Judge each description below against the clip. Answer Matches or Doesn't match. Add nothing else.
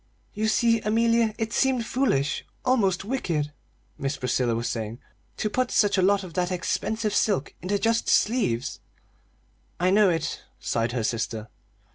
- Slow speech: Doesn't match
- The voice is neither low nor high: Doesn't match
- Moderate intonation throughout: Doesn't match